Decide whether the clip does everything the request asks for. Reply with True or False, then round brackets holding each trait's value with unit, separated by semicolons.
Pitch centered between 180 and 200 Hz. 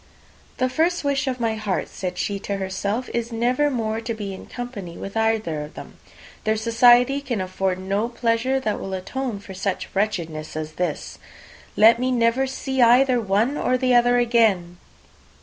False (225 Hz)